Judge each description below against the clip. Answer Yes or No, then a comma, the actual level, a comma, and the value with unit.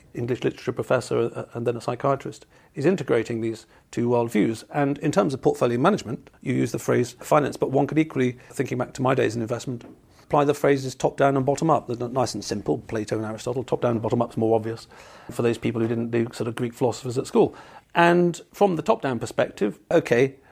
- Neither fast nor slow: No, fast, 210 wpm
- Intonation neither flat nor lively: Yes, average, 3.5 semitones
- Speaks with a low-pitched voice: Yes, low, 125 Hz